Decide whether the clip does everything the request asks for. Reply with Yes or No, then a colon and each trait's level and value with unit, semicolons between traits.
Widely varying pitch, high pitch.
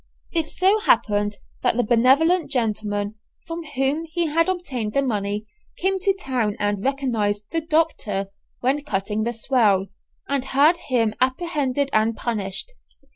Yes: wide, 7.1 semitones; very high, 255 Hz